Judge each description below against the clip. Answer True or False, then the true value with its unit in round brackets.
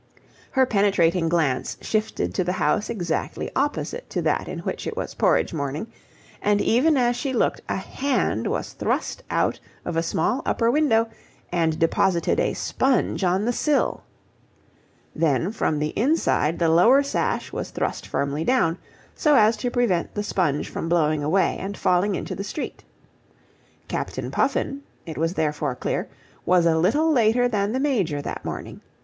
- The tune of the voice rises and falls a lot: True (6.9 semitones)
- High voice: True (195 Hz)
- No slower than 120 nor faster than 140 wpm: False (165 wpm)